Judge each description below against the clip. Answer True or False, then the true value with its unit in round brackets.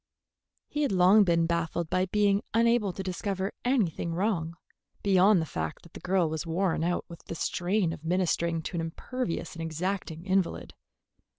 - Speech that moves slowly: False (170 wpm)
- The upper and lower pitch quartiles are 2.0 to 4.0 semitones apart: True (3.0 semitones)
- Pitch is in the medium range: True (180 Hz)